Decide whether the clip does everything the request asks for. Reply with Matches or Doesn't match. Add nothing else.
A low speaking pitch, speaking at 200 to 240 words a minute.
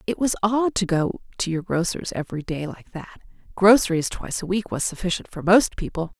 Doesn't match